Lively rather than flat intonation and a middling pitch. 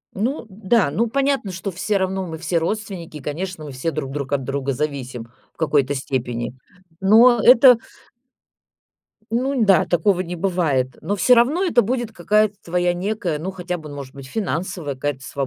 Yes: wide, 6.9 semitones; medium, 180 Hz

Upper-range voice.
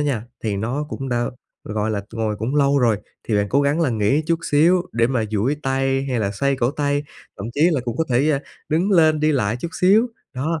No: low, 135 Hz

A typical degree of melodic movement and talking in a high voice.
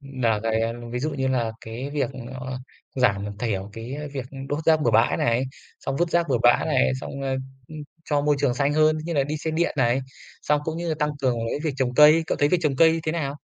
No: average, 4.0 semitones; low, 135 Hz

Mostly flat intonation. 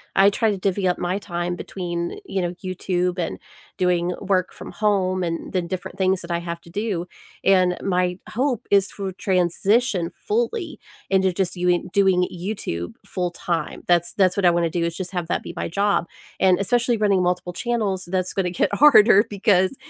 Yes: narrow, 2.3 semitones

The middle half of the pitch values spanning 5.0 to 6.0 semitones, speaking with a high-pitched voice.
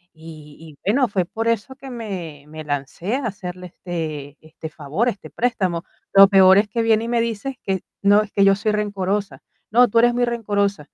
Yes: wide, 5.5 semitones; high, 200 Hz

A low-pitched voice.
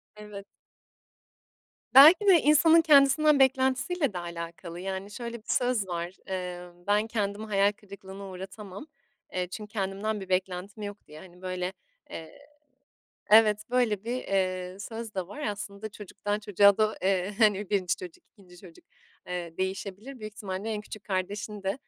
No: high, 200 Hz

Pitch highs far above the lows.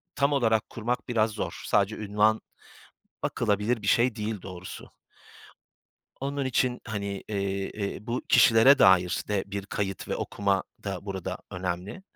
No: average, 3.1 semitones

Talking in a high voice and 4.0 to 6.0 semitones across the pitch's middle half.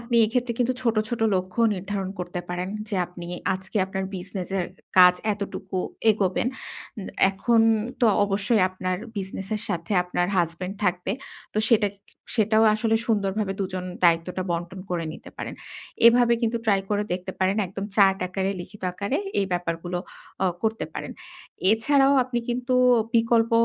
No: high, 195 Hz; average, 3.6 semitones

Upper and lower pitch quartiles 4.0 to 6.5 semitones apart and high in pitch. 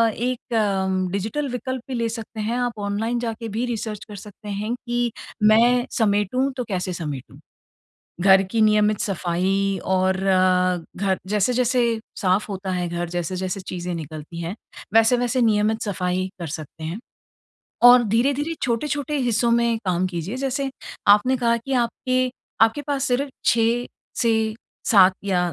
Yes: average, 4.3 semitones; high, 215 Hz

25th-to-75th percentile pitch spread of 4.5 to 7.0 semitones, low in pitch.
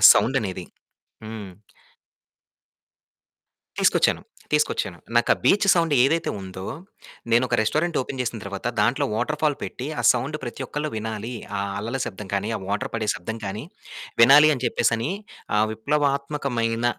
Yes: average, 4.9 semitones; low, 120 Hz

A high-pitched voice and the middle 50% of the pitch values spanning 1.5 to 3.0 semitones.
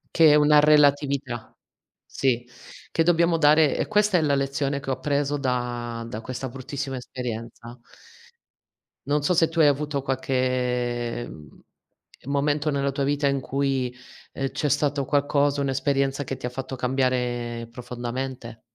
No: low, 135 Hz; average, 2.7 semitones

